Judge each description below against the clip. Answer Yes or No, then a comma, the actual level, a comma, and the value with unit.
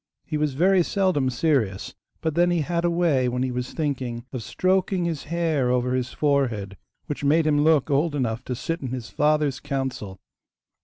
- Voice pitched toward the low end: No, medium, 145 Hz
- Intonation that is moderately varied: Yes, average, 4.5 semitones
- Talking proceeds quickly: No, average, 190 wpm